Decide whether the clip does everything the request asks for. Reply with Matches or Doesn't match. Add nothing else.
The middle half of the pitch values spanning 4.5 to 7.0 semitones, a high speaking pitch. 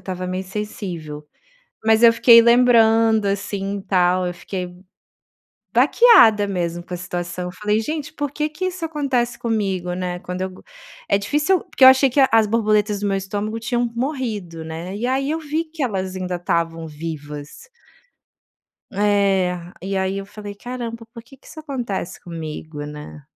Matches